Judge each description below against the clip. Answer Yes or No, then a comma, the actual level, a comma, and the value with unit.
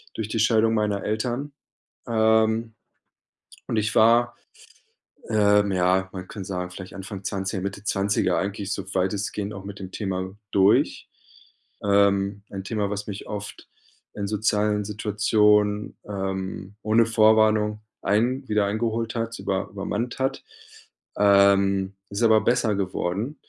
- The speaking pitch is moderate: No, low, 105 Hz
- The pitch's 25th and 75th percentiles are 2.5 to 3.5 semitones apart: No, narrow, 2.0 semitones